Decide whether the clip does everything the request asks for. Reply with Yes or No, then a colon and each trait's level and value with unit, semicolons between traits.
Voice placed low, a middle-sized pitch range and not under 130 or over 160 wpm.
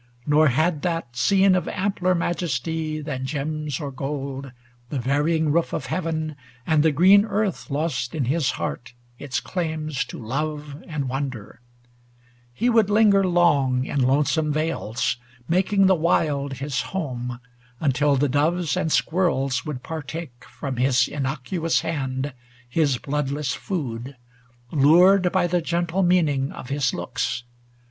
No: medium, 150 Hz; average, 4.0 semitones; average, 140 wpm